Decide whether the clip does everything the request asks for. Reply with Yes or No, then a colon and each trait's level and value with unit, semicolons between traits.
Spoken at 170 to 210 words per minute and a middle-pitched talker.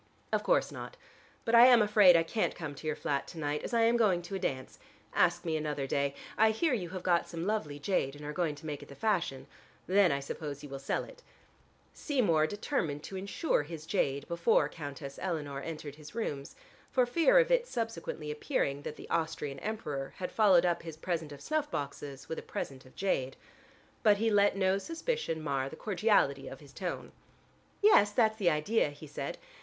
Yes: fast, 205 wpm; medium, 170 Hz